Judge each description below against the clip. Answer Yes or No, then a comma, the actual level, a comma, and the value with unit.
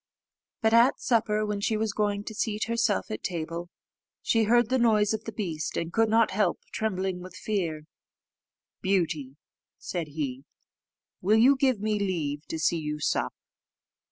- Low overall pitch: No, high, 205 Hz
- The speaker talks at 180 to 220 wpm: No, average, 160 wpm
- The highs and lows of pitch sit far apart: No, average, 4.8 semitones